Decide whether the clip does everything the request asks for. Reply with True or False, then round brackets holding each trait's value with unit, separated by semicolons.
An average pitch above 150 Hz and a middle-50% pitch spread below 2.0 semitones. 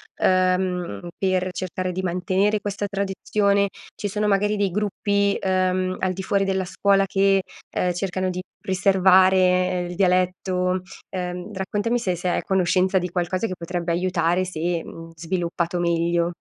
True (185 Hz; 1.6 semitones)